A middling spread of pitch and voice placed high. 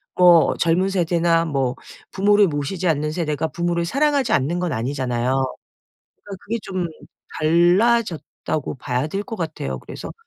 No: average, 4.5 semitones; medium, 170 Hz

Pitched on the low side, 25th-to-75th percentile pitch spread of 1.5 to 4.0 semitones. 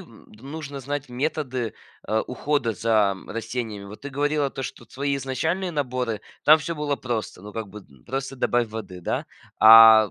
No: low, 125 Hz; average, 4.5 semitones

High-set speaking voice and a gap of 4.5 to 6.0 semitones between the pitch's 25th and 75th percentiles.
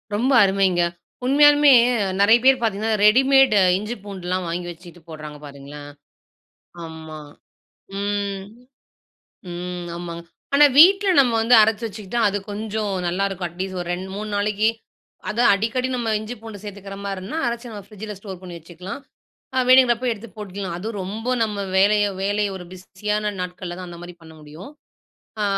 No: high, 200 Hz; average, 3.7 semitones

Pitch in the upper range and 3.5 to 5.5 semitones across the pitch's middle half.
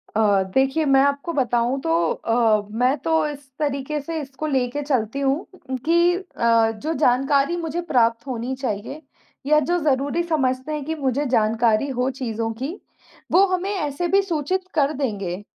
Yes: very high, 275 Hz; average, 4.3 semitones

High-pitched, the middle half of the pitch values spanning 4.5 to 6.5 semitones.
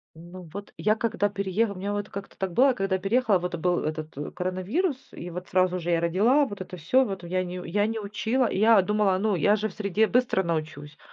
No: high, 195 Hz; average, 3.2 semitones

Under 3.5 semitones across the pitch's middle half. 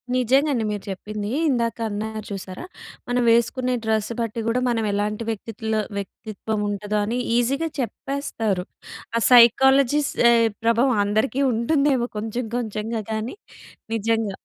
Yes: average, 2.7 semitones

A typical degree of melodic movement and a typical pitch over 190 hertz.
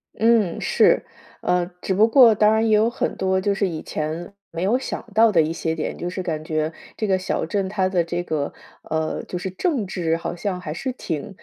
No: average, 4.3 semitones; medium, 185 Hz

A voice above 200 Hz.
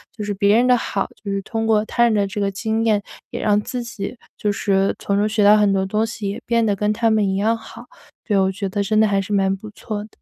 Yes: high, 210 Hz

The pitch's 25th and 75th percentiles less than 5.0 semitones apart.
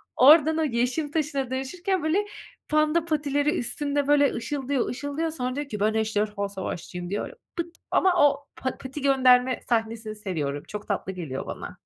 No: wide, 5.4 semitones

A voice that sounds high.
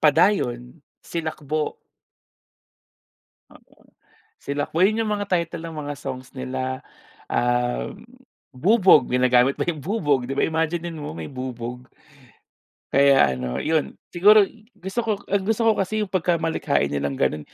No: medium, 150 Hz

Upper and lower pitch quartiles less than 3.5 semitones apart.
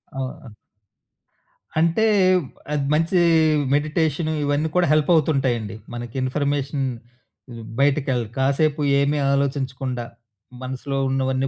Yes: narrow, 2.6 semitones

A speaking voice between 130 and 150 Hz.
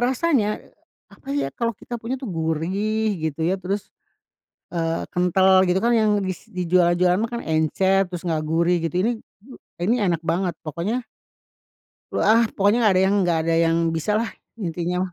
No: medium, 185 Hz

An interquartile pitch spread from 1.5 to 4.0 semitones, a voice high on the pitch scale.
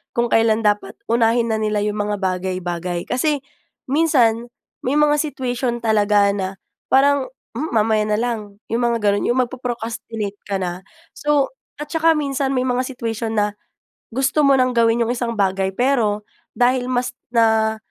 Yes: average, 3.5 semitones; high, 230 Hz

